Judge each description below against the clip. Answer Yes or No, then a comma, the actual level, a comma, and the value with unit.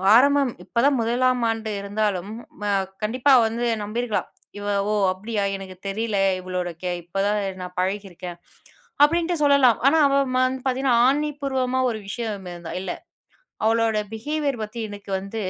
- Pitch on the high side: Yes, high, 225 Hz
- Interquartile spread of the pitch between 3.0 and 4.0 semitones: No, average, 4.4 semitones